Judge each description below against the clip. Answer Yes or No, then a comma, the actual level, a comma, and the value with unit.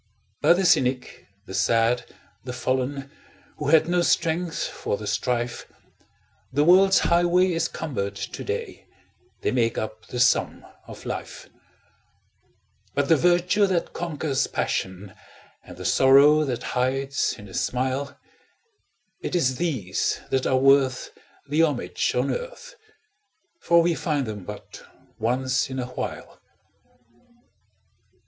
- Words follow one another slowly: Yes, slow, 130 wpm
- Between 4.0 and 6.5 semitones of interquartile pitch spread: Yes, average, 5.1 semitones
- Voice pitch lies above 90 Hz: Yes, low, 135 Hz